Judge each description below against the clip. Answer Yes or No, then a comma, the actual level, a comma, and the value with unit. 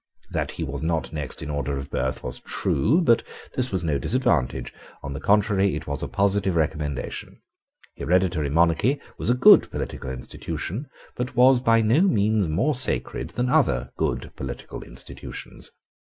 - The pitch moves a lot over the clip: Yes, wide, 8.6 semitones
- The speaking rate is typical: Yes, average, 160 wpm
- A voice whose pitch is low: Yes, very low, 95 Hz